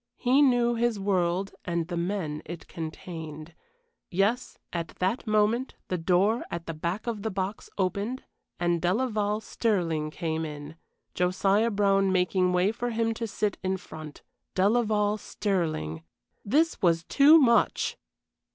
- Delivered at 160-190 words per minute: No, average, 140 wpm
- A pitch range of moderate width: Yes, average, 4.5 semitones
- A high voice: Yes, high, 195 Hz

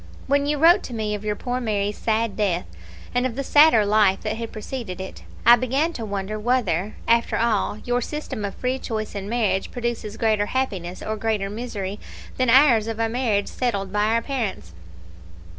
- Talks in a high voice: Yes, high, 225 Hz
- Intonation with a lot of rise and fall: No, average, 3.2 semitones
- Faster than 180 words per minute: Yes, average, 190 wpm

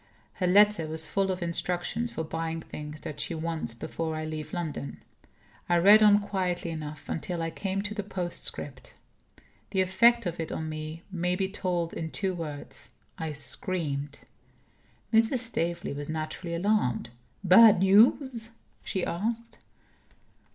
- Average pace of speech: Yes, average, 145 wpm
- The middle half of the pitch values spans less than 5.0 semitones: Yes, average, 3.8 semitones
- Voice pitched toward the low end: No, medium, 175 Hz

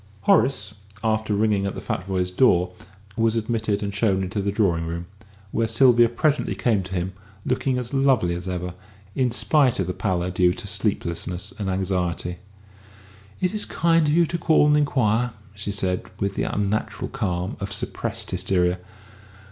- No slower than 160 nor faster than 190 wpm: Yes, average, 165 wpm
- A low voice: Yes, low, 100 Hz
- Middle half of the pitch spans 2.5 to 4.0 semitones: No, average, 4.8 semitones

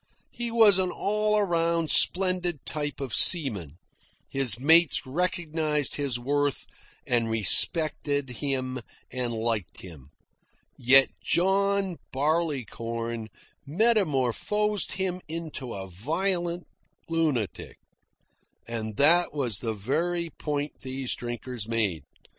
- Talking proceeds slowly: Yes, slow, 100 wpm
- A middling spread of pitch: No, wide, 6.5 semitones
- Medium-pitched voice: Yes, medium, 145 Hz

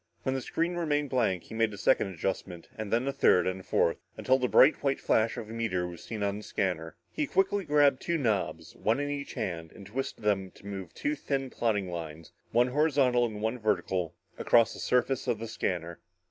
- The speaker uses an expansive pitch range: Yes, wide, 6.2 semitones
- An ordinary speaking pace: No, fast, 215 wpm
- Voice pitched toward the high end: No, low, 110 Hz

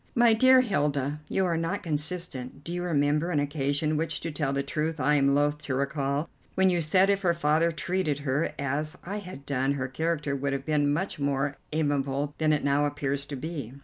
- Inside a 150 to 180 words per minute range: No, fast, 205 wpm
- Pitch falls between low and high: Yes, medium, 150 Hz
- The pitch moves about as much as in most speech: Yes, average, 3.1 semitones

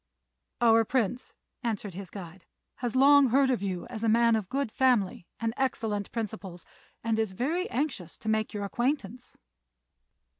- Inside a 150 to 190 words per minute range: Yes, average, 155 wpm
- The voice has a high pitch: Yes, high, 225 Hz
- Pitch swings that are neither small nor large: Yes, average, 4.1 semitones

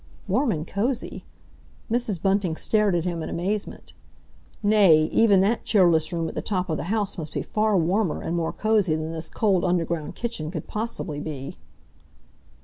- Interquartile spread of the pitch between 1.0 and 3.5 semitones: No, average, 4.6 semitones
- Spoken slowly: No, average, 170 wpm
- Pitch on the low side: No, medium, 185 Hz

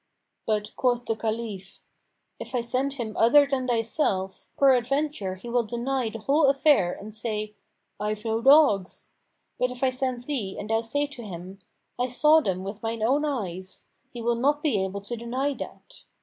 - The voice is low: No, high, 235 Hz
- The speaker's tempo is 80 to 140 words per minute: No, average, 180 wpm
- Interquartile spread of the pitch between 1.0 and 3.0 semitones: No, average, 4.2 semitones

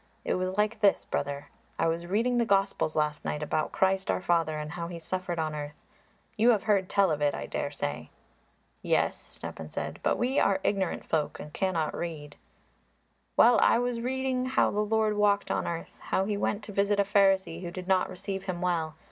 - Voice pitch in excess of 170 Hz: Yes, high, 190 Hz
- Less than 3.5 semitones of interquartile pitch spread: No, average, 4.1 semitones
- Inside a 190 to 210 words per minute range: Yes, average, 200 wpm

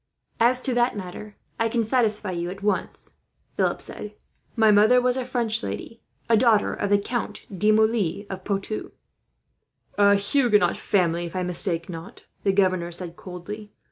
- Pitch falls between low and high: No, high, 210 Hz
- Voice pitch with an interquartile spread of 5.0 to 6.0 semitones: No, average, 3.6 semitones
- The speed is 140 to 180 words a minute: Yes, average, 165 wpm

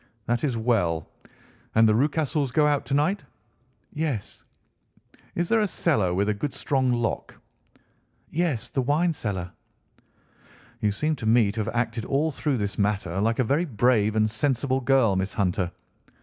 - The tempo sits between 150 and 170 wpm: Yes, average, 165 wpm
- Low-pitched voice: Yes, low, 120 Hz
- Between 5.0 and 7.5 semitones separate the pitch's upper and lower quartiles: Yes, wide, 5.5 semitones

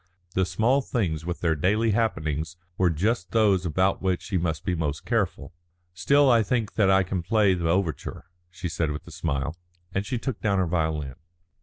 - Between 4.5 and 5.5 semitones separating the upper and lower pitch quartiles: Yes, average, 4.8 semitones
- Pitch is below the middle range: Yes, very low, 90 Hz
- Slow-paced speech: No, average, 190 wpm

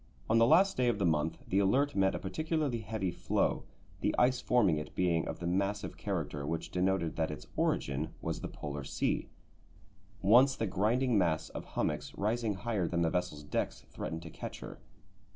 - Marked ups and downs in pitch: Yes, wide, 6.0 semitones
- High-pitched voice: No, very low, 95 Hz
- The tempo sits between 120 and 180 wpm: No, average, 190 wpm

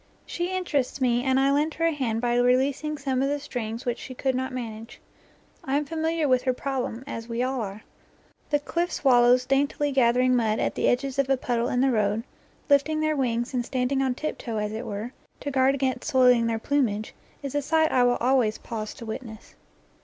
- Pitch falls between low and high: No, very high, 255 Hz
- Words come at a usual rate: No, fast, 210 wpm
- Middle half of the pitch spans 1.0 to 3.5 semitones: Yes, average, 2.9 semitones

